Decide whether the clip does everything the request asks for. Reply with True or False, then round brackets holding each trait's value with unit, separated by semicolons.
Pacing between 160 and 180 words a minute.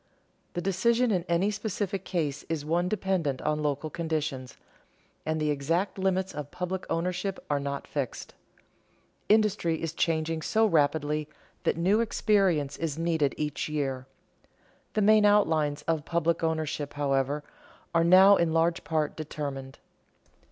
False (135 wpm)